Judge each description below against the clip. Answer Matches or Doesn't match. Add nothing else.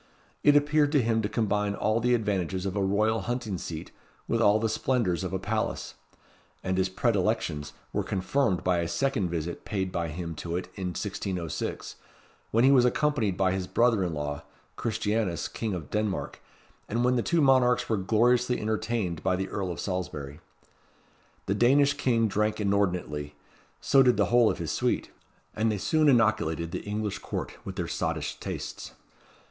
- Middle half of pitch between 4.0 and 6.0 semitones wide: Matches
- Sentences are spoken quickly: Doesn't match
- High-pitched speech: Doesn't match